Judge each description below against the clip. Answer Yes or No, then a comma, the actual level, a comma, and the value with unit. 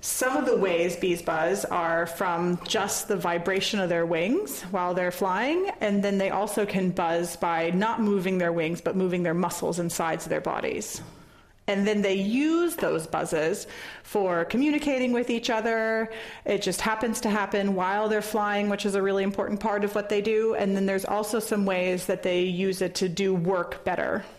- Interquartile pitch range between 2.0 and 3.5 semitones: Yes, average, 3.1 semitones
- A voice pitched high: Yes, high, 195 Hz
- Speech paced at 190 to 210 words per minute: Yes, average, 195 wpm